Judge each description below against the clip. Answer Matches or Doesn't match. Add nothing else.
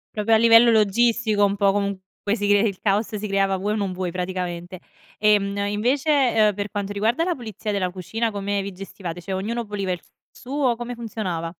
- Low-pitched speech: Doesn't match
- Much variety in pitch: Doesn't match